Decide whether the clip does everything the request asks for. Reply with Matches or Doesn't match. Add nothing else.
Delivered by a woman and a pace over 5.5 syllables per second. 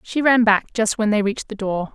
Matches